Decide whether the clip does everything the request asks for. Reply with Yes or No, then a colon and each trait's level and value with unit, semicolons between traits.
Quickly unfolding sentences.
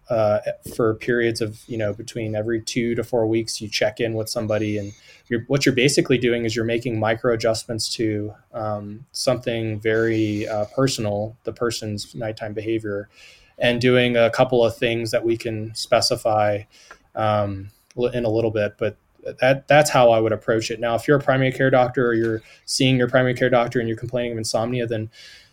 No: average, 185 wpm